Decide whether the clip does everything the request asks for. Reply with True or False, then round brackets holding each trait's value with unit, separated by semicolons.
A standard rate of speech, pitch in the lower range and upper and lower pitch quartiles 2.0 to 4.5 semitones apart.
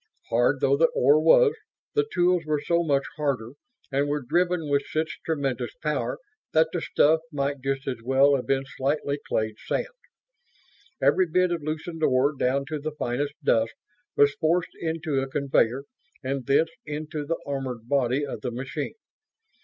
False (165 wpm; 145 Hz; 3.0 semitones)